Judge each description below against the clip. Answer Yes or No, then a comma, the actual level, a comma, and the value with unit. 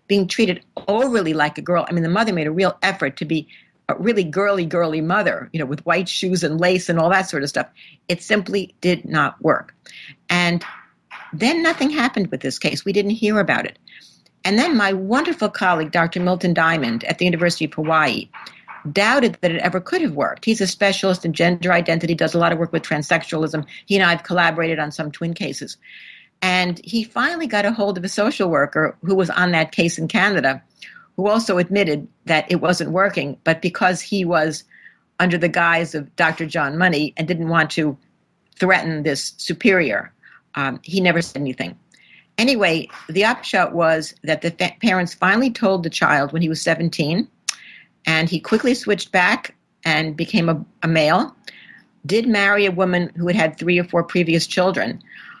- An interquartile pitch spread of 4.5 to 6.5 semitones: No, average, 3.6 semitones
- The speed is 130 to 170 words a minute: No, average, 195 wpm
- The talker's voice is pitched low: No, medium, 175 Hz